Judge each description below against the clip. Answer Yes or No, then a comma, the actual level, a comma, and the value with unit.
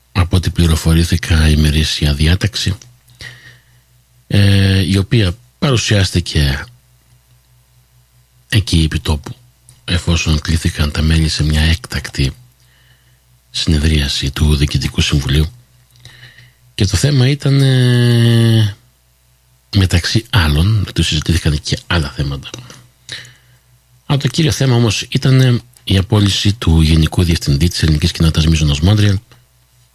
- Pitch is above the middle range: No, low, 100 Hz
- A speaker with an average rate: No, slow, 95 wpm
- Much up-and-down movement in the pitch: Yes, wide, 7.7 semitones